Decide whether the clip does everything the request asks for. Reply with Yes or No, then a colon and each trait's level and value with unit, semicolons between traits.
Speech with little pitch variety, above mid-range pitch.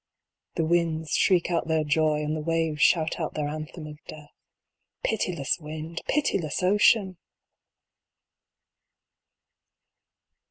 No: narrow, 2.0 semitones; medium, 160 Hz